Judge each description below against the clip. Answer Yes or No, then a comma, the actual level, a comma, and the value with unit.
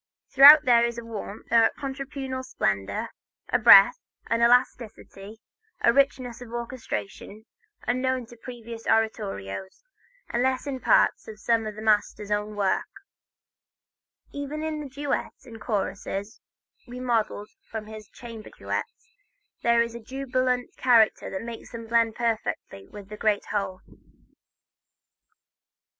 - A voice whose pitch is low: No, high, 230 Hz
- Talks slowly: Yes, slow, 125 wpm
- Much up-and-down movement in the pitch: No, average, 3.1 semitones